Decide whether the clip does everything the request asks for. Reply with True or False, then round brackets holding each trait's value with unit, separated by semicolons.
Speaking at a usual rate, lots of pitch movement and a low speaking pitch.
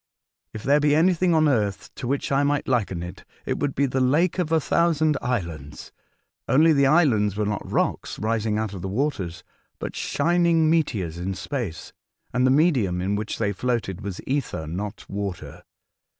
True (180 wpm; 6.8 semitones; 125 Hz)